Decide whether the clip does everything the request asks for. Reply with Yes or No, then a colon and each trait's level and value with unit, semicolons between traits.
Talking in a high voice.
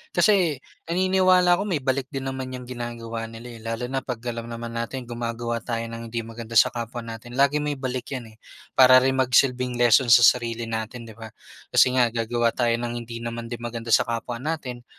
No: low, 120 Hz